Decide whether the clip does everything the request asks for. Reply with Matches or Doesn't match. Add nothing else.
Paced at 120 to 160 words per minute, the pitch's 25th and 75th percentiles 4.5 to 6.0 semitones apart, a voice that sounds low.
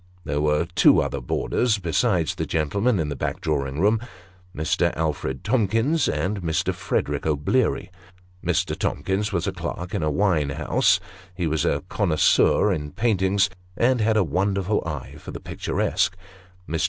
Matches